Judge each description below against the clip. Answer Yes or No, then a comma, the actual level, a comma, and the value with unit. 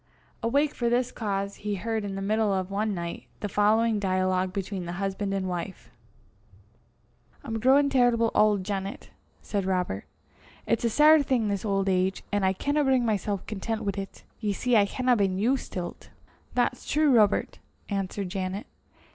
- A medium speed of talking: Yes, average, 170 wpm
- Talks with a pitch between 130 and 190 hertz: No, high, 205 Hz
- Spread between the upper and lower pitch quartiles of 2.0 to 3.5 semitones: Yes, average, 3.2 semitones